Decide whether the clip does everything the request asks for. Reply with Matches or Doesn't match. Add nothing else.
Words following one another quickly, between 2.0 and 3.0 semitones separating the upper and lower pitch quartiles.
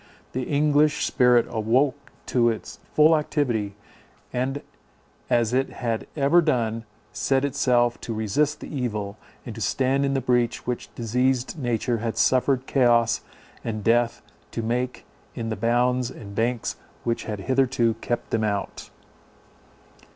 Doesn't match